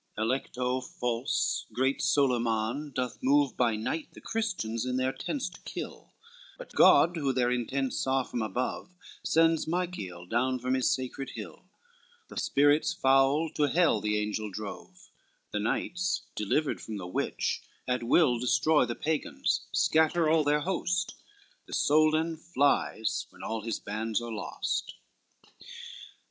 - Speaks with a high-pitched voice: No, low, 130 Hz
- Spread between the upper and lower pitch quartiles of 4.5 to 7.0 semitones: Yes, average, 5.2 semitones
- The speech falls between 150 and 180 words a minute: No, average, 140 wpm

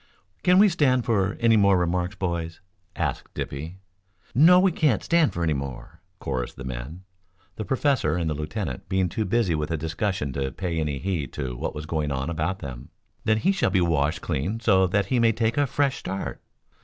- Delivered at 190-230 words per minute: Yes, average, 200 wpm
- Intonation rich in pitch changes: Yes, wide, 6.9 semitones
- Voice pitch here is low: Yes, very low, 90 Hz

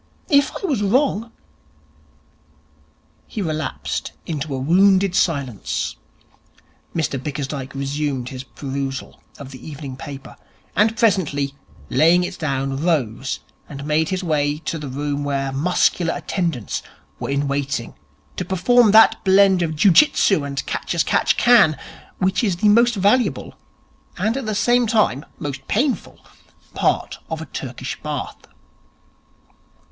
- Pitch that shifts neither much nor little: No, wide, 6.3 semitones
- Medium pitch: Yes, medium, 155 Hz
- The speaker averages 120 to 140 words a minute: Yes, slow, 135 wpm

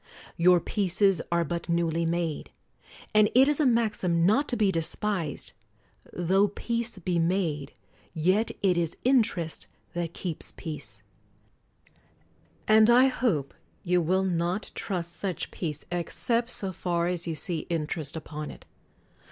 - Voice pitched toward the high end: No, medium, 175 Hz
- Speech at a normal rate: Yes, average, 145 wpm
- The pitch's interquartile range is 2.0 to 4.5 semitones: Yes, average, 3.9 semitones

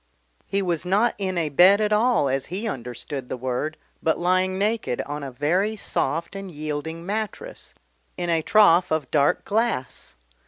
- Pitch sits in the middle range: Yes, medium, 175 Hz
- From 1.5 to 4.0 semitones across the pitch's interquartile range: No, average, 5.3 semitones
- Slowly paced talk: No, average, 165 wpm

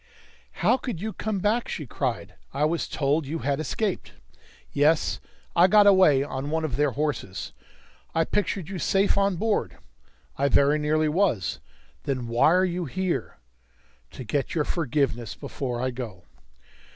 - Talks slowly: No, average, 155 wpm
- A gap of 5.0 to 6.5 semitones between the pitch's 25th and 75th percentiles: Yes, wide, 5.4 semitones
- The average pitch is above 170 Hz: No, medium, 155 Hz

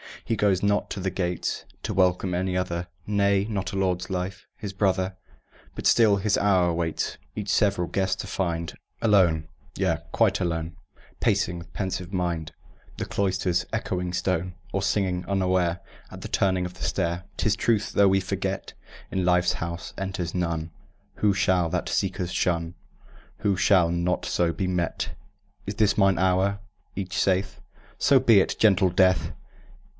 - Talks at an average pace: Yes, average, 160 wpm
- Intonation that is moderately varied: No, narrow, 2.0 semitones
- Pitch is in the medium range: No, very low, 95 Hz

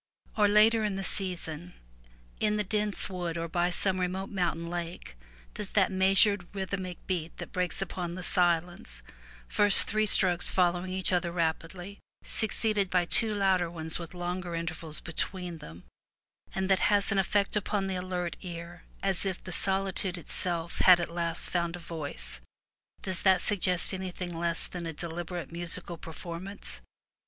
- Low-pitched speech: No, medium, 180 Hz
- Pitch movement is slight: Yes, narrow, 2.2 semitones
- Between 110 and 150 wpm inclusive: No, average, 165 wpm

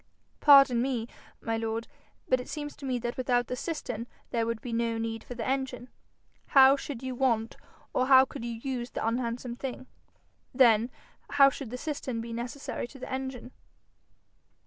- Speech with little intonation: Yes, narrow, 2.3 semitones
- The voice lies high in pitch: Yes, high, 245 Hz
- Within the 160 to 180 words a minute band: Yes, average, 175 wpm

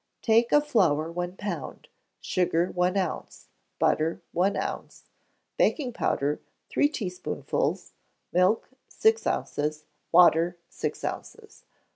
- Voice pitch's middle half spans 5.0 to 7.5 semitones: Yes, wide, 5.5 semitones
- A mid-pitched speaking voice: Yes, medium, 180 Hz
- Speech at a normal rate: No, slow, 105 wpm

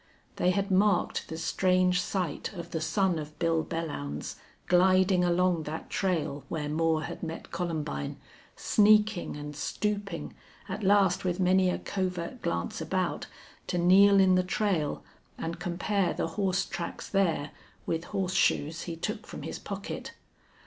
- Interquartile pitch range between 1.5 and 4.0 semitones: Yes, average, 2.8 semitones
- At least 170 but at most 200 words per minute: No, average, 145 wpm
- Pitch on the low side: No, medium, 180 Hz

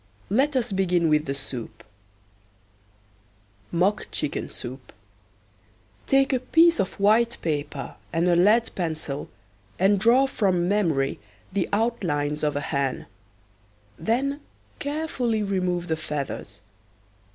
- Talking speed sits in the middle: No, slow, 115 wpm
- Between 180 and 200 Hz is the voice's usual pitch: Yes, medium, 185 Hz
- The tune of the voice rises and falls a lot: Yes, wide, 7.3 semitones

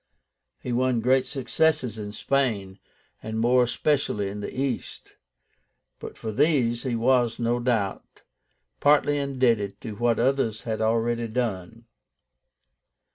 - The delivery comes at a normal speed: No, slow, 125 wpm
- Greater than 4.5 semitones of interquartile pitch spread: No, average, 2.8 semitones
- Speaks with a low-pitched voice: Yes, low, 120 Hz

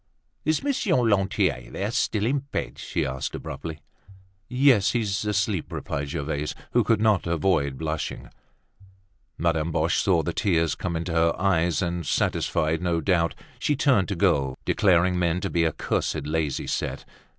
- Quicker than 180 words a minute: No, average, 155 wpm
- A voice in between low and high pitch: No, very low, 85 Hz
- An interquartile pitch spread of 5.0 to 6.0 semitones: No, average, 4.3 semitones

